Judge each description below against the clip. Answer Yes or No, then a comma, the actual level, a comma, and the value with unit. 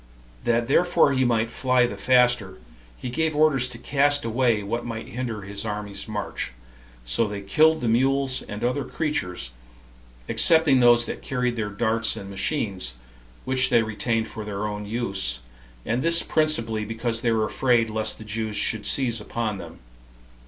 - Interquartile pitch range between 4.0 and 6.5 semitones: No, average, 3.4 semitones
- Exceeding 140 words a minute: Yes, average, 165 wpm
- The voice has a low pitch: Yes, low, 115 Hz